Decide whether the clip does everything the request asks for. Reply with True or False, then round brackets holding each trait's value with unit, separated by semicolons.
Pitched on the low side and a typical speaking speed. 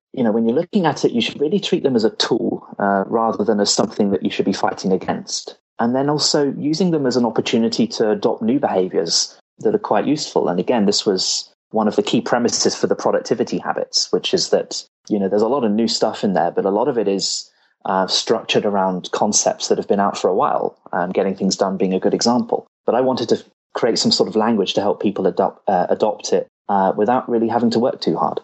False (120 Hz; 245 wpm)